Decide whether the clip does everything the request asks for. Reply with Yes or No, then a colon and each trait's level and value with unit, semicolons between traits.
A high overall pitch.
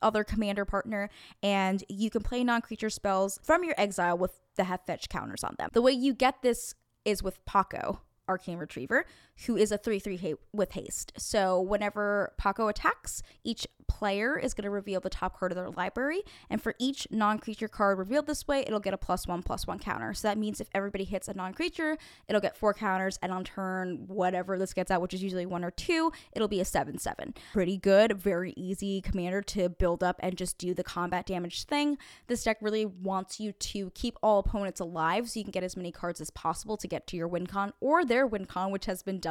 Yes: high, 200 Hz